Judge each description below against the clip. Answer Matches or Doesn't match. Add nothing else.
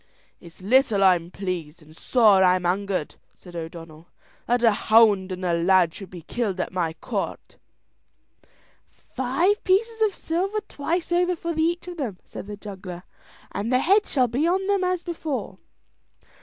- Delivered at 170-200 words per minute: Doesn't match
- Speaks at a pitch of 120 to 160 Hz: Doesn't match